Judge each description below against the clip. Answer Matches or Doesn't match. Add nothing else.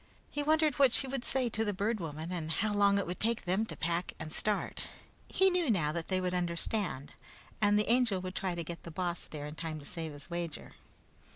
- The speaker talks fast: Matches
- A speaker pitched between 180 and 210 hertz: Matches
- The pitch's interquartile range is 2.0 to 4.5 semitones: Doesn't match